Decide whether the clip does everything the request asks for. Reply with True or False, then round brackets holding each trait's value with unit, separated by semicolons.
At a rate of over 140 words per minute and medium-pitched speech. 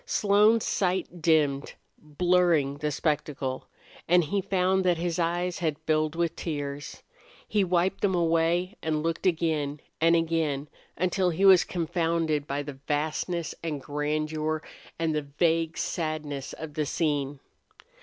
False (135 wpm; 160 Hz)